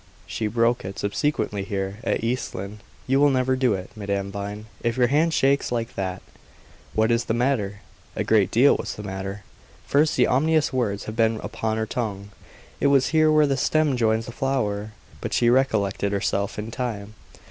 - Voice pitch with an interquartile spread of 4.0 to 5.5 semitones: Yes, average, 4.4 semitones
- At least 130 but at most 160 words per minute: No, average, 190 wpm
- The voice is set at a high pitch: No, low, 115 Hz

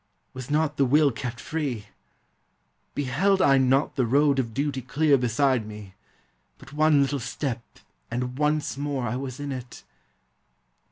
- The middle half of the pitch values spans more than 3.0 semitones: No, average, 2.7 semitones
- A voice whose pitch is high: No, low, 135 Hz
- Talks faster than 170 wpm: No, average, 155 wpm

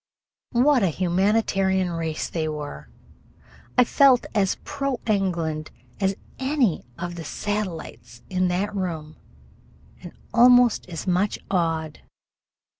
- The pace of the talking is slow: Yes, slow, 115 wpm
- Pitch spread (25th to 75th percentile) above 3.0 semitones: Yes, average, 4.9 semitones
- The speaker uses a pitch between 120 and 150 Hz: No, medium, 185 Hz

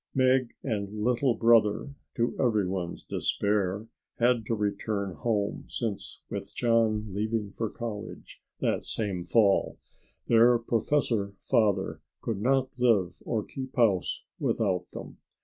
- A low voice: Yes, low, 110 Hz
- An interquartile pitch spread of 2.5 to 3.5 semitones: Yes, average, 2.8 semitones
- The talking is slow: Yes, slow, 120 wpm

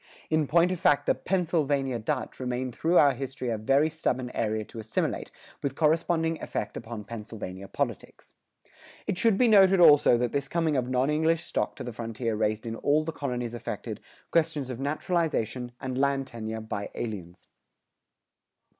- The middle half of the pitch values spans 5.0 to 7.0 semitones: Yes, wide, 5.5 semitones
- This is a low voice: Yes, low, 130 Hz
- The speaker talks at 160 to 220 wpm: Yes, average, 165 wpm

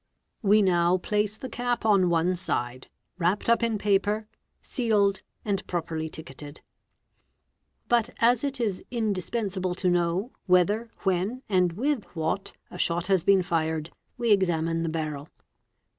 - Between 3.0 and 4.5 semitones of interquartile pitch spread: Yes, average, 4.1 semitones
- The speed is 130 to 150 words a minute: Yes, average, 145 wpm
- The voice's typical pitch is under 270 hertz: Yes, high, 190 Hz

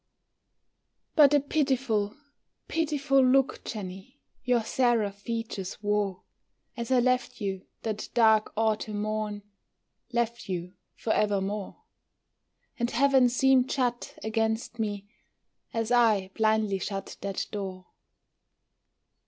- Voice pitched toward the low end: No, high, 220 Hz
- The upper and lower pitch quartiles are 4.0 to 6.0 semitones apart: No, average, 3.5 semitones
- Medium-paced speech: No, slow, 105 wpm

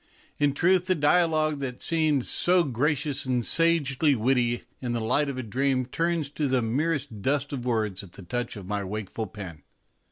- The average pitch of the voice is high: No, low, 135 Hz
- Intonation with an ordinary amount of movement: Yes, average, 4.5 semitones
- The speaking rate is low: No, average, 185 wpm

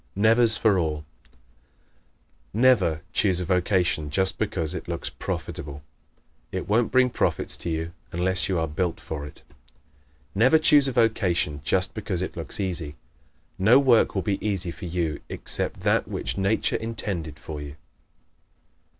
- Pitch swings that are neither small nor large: Yes, average, 5.0 semitones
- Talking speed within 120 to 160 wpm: Yes, average, 155 wpm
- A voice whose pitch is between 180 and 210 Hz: No, very low, 95 Hz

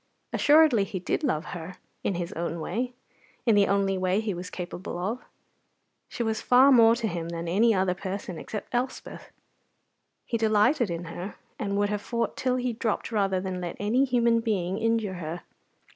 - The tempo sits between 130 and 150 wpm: No, average, 180 wpm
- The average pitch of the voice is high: Yes, high, 205 Hz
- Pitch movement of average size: Yes, average, 4.3 semitones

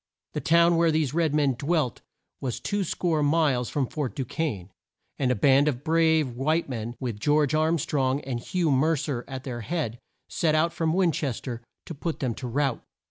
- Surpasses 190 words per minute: Yes, average, 200 wpm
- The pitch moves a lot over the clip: No, average, 4.1 semitones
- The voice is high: No, medium, 145 Hz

